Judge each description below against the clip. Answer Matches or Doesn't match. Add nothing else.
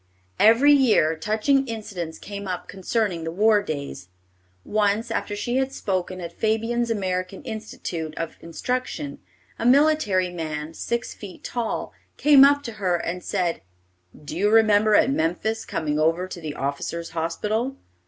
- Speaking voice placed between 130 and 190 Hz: Doesn't match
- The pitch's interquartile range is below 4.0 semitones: Doesn't match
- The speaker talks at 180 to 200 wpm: Doesn't match